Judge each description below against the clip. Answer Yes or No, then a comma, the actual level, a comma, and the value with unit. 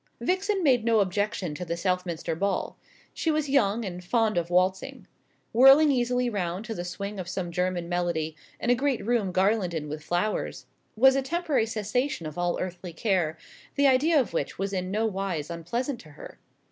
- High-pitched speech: Yes, high, 195 Hz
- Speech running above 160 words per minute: Yes, average, 185 wpm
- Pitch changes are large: Yes, wide, 5.8 semitones